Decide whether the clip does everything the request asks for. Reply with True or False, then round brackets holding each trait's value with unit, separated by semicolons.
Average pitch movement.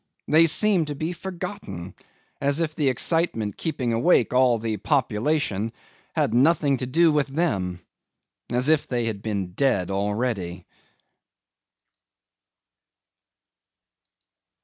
False (6.7 semitones)